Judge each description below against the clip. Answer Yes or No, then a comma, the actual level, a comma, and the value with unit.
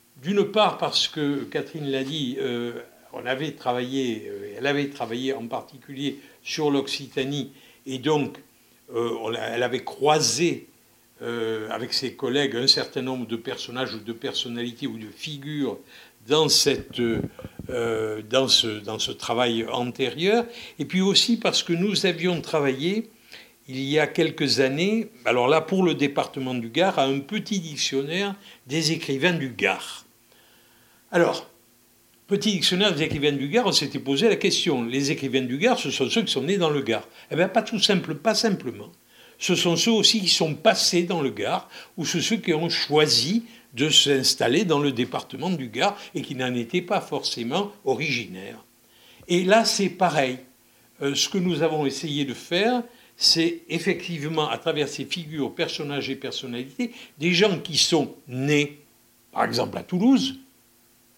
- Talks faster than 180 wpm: No, average, 165 wpm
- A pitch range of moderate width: No, wide, 5.9 semitones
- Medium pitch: Yes, medium, 145 Hz